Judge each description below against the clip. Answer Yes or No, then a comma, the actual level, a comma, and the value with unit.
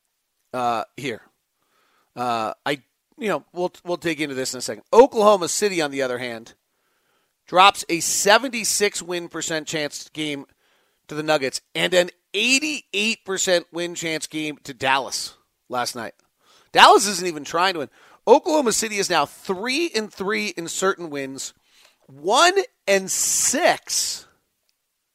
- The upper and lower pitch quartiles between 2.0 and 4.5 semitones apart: No, average, 5.3 semitones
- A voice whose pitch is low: No, medium, 180 Hz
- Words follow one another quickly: No, average, 145 wpm